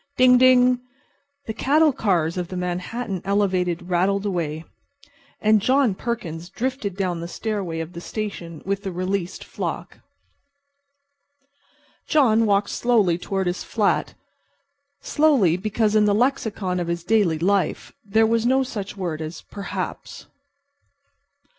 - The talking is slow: Yes, slow, 130 wpm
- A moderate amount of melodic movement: Yes, average, 4.3 semitones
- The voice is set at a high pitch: Yes, high, 200 Hz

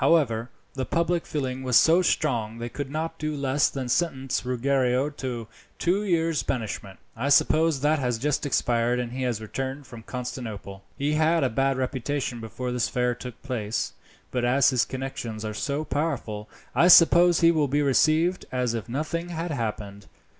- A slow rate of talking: No, average, 175 wpm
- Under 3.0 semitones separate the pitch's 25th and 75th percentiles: No, average, 4.2 semitones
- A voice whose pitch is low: Yes, low, 130 Hz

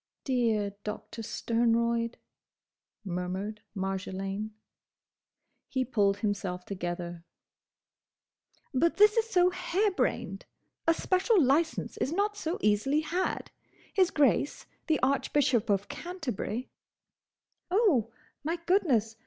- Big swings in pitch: Yes, wide, 8.7 semitones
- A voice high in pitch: Yes, high, 245 Hz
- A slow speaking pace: Yes, slow, 95 wpm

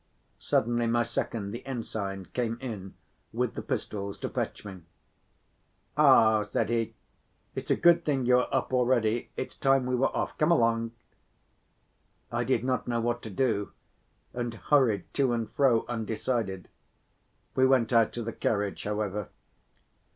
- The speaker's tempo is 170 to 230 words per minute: No, average, 150 wpm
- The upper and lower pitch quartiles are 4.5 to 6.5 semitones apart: No, average, 2.8 semitones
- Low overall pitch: Yes, low, 115 Hz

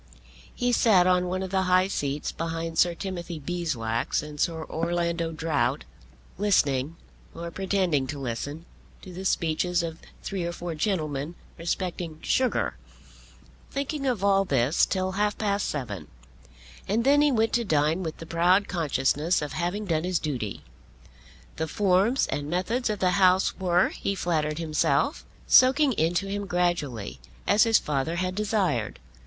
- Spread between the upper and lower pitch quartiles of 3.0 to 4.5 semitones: Yes, average, 3.9 semitones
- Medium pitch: Yes, medium, 175 Hz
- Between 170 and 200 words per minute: No, average, 150 wpm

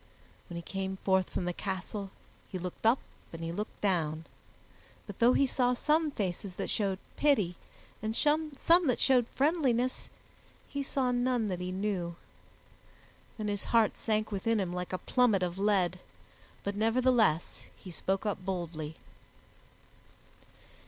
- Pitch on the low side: No, high, 205 Hz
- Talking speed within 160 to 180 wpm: No, average, 145 wpm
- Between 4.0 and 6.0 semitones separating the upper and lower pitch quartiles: Yes, average, 5.1 semitones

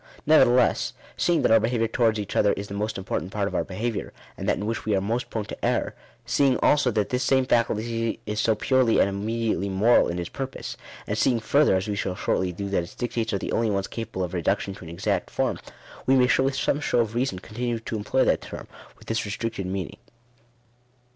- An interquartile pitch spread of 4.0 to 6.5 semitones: No, average, 3.4 semitones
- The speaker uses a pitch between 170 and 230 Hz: No, low, 110 Hz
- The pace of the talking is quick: Yes, fast, 225 wpm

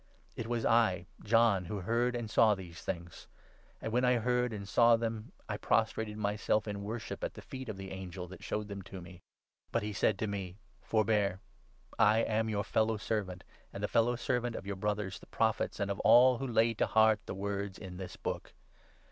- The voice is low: Yes, low, 105 Hz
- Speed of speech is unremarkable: No, fast, 215 wpm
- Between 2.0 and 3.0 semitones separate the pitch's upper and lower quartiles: Yes, average, 2.7 semitones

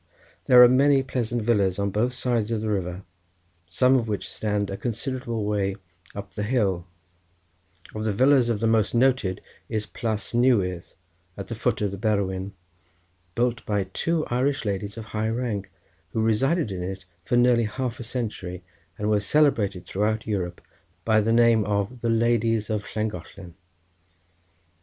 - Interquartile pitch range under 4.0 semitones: Yes, average, 3.1 semitones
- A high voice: No, low, 110 Hz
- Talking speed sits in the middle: Yes, average, 160 wpm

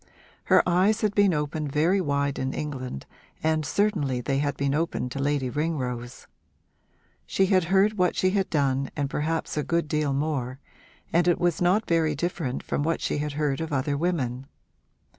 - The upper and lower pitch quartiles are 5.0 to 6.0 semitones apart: No, average, 4.0 semitones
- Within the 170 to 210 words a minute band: Yes, average, 180 wpm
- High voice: No, medium, 150 Hz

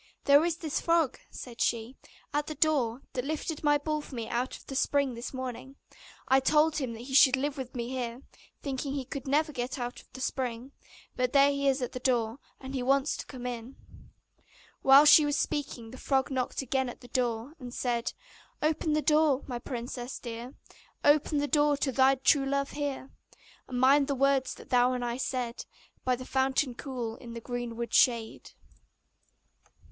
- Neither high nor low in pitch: No, very high, 265 Hz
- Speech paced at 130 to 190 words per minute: No, average, 200 wpm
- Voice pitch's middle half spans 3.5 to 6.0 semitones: No, narrow, 2.6 semitones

